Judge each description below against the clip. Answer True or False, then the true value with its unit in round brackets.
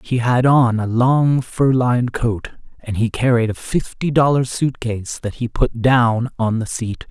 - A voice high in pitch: False (120 Hz)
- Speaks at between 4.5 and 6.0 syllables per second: False (4.1 syllables/s)